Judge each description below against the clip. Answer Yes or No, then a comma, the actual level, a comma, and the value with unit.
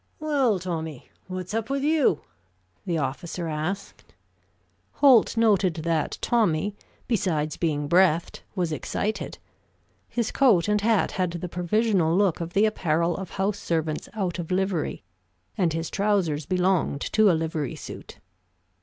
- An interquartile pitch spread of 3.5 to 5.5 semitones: Yes, average, 4.3 semitones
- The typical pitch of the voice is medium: Yes, medium, 180 Hz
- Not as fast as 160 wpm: Yes, slow, 135 wpm